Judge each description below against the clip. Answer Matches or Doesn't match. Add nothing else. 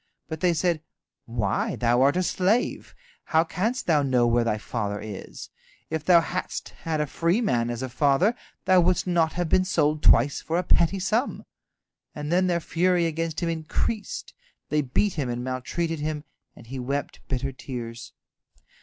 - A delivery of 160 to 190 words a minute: Matches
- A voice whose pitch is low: Doesn't match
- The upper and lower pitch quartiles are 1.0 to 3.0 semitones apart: Doesn't match